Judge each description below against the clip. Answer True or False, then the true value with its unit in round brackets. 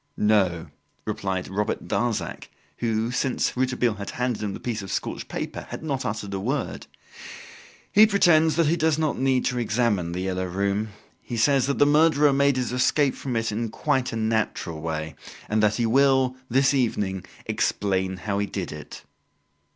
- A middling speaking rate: True (175 wpm)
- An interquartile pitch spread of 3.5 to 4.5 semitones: False (5.2 semitones)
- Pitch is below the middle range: True (115 Hz)